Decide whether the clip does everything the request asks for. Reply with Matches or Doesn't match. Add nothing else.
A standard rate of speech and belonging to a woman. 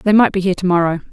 Doesn't match